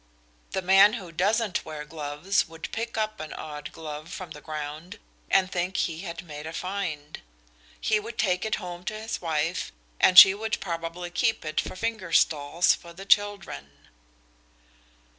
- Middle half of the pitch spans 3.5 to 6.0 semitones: Yes, average, 4.2 semitones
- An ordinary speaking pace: Yes, average, 165 wpm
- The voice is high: No, medium, 175 Hz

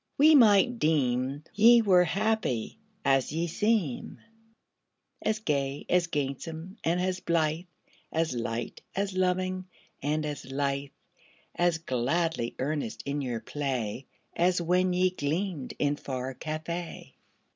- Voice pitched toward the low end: No, medium, 160 Hz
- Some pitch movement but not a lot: Yes, average, 5.0 semitones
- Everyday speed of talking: No, slow, 125 wpm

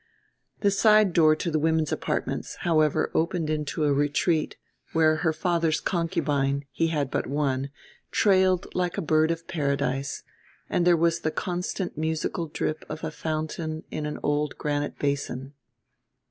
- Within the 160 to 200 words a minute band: No, average, 150 wpm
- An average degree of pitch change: No, narrow, 2.3 semitones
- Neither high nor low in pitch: Yes, medium, 155 Hz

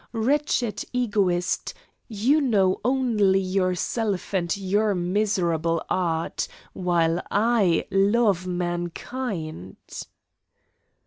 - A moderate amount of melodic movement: Yes, average, 4.2 semitones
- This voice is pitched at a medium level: No, high, 195 Hz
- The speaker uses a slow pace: Yes, slow, 75 wpm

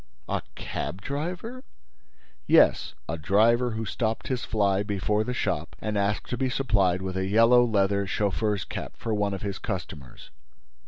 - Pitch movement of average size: Yes, average, 3.4 semitones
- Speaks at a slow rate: No, average, 160 wpm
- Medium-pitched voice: No, low, 105 Hz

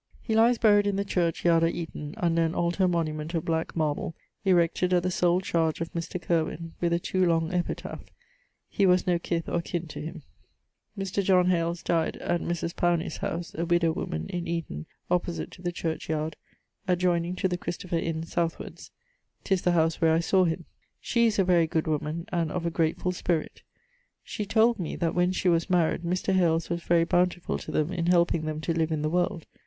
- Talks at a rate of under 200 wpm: No, fast, 205 wpm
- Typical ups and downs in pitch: No, narrow, 1.7 semitones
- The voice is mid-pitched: Yes, medium, 170 Hz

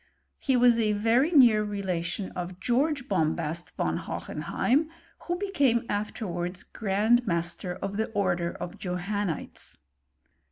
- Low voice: No, high, 205 Hz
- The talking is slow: Yes, slow, 120 wpm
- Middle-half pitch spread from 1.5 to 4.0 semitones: No, average, 5.3 semitones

